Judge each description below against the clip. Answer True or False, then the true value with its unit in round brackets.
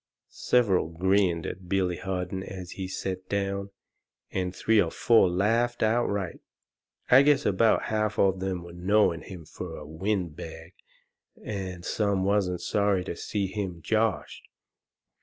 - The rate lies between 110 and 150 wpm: True (140 wpm)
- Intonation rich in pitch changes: False (2.5 semitones)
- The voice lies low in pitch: True (95 Hz)